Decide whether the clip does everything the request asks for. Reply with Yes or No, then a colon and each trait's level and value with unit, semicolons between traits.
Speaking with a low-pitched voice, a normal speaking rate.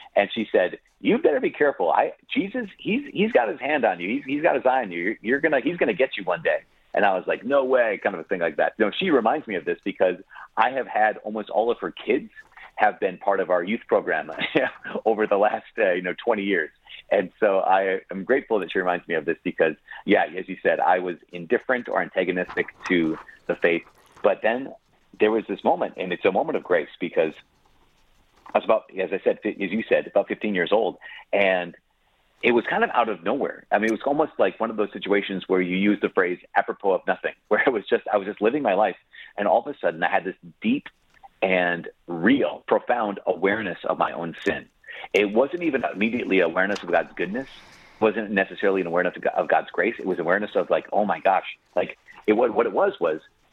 No: low, 105 Hz; fast, 235 wpm